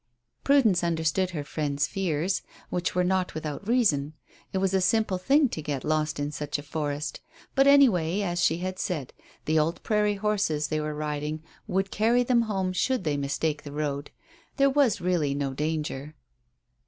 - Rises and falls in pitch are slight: No, average, 4.8 semitones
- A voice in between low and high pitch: Yes, medium, 170 Hz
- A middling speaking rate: Yes, average, 175 wpm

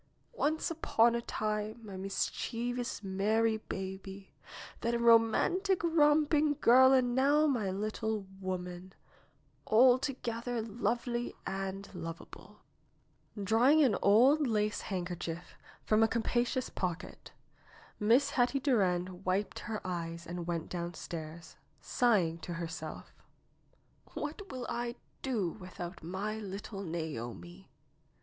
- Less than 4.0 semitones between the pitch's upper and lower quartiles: No, average, 5.0 semitones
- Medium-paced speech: No, slow, 110 wpm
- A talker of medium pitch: No, high, 215 Hz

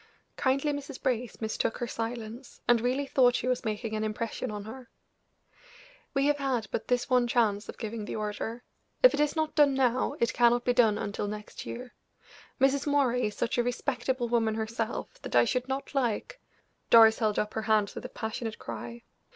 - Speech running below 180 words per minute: No, average, 195 wpm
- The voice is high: Yes, high, 240 Hz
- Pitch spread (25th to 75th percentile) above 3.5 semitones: No, average, 2.9 semitones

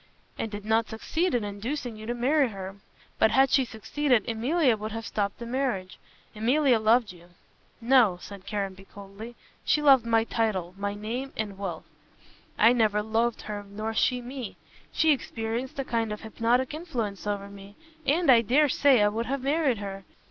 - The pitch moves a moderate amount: Yes, average, 3.9 semitones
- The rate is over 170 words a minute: Yes, average, 180 wpm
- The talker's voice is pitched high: Yes, high, 225 Hz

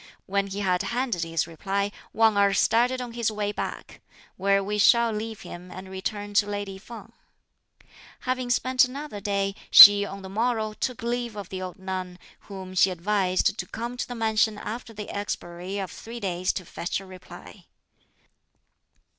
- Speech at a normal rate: Yes, average, 170 wpm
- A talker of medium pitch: No, high, 205 Hz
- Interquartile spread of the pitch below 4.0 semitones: Yes, average, 3.1 semitones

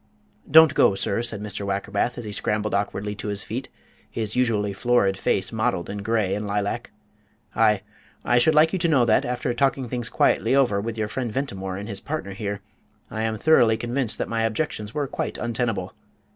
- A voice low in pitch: Yes, low, 110 Hz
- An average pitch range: Yes, average, 3.2 semitones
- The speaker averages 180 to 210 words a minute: Yes, average, 200 wpm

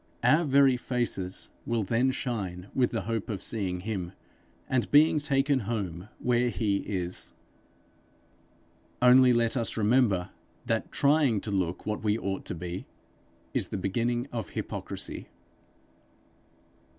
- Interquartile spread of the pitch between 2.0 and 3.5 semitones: No, average, 4.4 semitones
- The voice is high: No, low, 115 Hz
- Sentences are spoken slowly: Yes, slow, 130 wpm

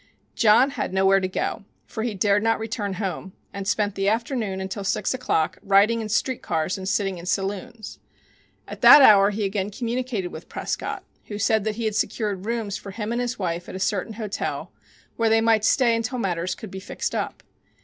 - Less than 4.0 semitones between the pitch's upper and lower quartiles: Yes, average, 2.8 semitones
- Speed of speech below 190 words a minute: No, average, 200 wpm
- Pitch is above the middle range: Yes, high, 205 Hz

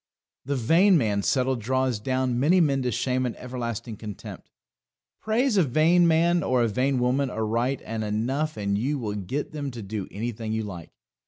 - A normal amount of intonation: Yes, average, 4.4 semitones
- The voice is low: Yes, low, 125 Hz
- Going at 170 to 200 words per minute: Yes, average, 180 wpm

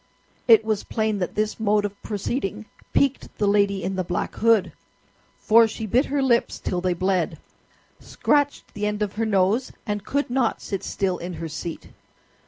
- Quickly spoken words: No, average, 180 wpm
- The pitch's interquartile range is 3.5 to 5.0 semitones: No, average, 2.9 semitones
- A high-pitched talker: Yes, high, 210 Hz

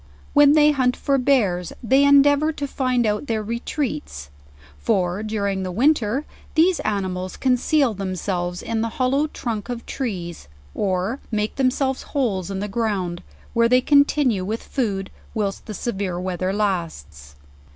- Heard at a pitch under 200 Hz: No, high, 220 Hz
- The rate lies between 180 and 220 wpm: No, average, 150 wpm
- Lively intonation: Yes, wide, 6.0 semitones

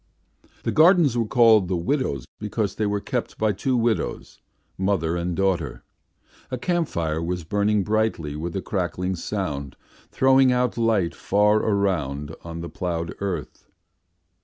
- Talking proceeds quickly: No, average, 145 wpm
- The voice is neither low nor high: No, low, 100 Hz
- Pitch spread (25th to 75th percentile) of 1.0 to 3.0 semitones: No, average, 4.8 semitones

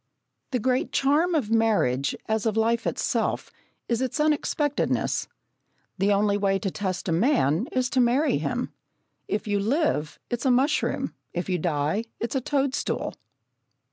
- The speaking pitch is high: Yes, high, 225 Hz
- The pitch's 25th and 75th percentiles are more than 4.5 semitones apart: Yes, average, 5.2 semitones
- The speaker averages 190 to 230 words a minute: No, average, 150 wpm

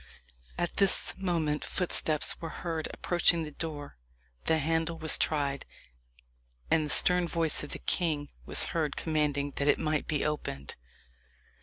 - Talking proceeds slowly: No, average, 145 wpm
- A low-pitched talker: No, medium, 155 Hz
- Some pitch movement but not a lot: No, narrow, 2.1 semitones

